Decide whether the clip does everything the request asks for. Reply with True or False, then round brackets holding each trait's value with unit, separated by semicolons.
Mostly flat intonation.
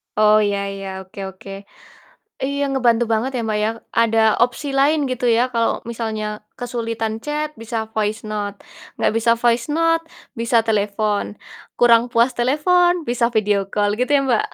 False (3.2 semitones)